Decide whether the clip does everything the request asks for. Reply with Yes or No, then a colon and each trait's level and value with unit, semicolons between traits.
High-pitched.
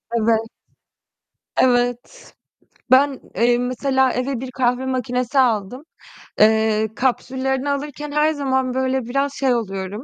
Yes: very high, 255 Hz